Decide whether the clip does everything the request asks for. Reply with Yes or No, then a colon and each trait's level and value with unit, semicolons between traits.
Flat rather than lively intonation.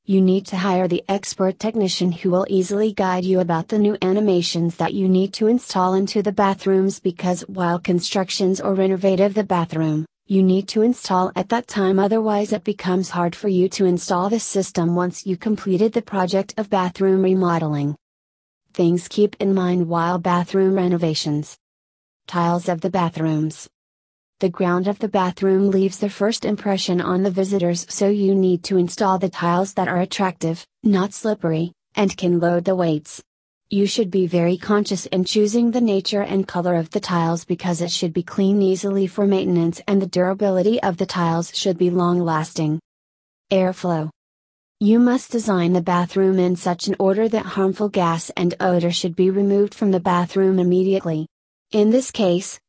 Yes: narrow, 2.2 semitones